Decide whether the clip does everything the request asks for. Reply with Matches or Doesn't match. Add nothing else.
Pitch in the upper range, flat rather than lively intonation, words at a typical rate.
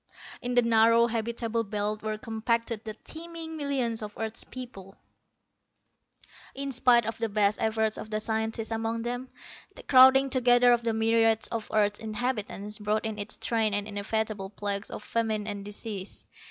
Matches